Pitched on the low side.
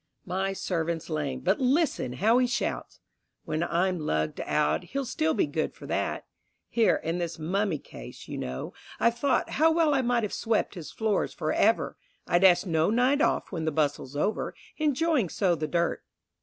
No: medium, 185 Hz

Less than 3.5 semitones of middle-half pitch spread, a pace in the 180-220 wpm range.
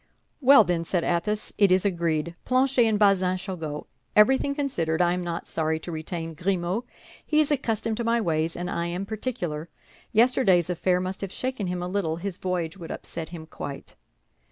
No: average, 4.3 semitones; average, 185 wpm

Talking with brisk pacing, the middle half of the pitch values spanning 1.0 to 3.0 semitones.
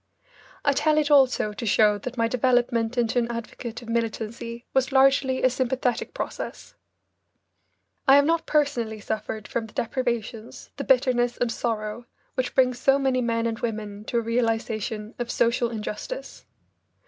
No: average, 155 wpm; narrow, 2.4 semitones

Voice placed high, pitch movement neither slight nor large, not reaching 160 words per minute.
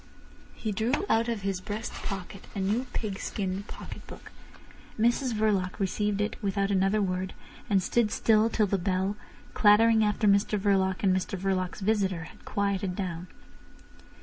No: high, 200 Hz; narrow, 2.2 semitones; average, 150 wpm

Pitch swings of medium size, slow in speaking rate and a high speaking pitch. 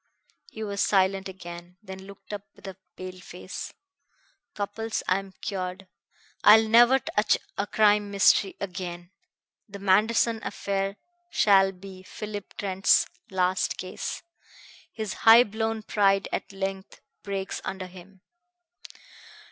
No: narrow, 1.7 semitones; slow, 125 wpm; high, 195 Hz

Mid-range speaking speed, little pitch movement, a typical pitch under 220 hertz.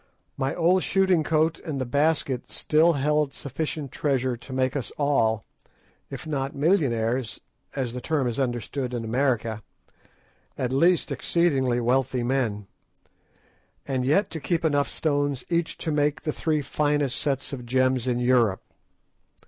No: average, 145 wpm; average, 3.4 semitones; low, 135 Hz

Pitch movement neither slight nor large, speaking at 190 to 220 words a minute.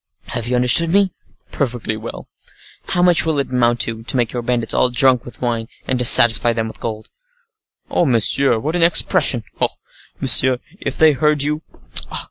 No: average, 4.1 semitones; average, 180 wpm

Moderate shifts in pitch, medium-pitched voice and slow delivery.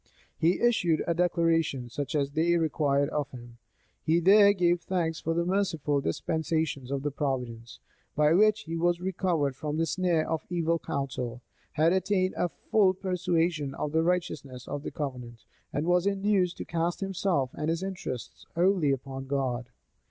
No: average, 4.2 semitones; medium, 165 Hz; average, 160 wpm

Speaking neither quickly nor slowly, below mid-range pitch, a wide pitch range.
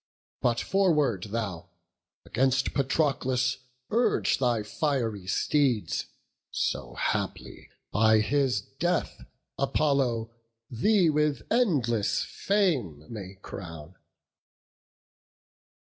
No: slow, 80 wpm; low, 125 Hz; wide, 5.8 semitones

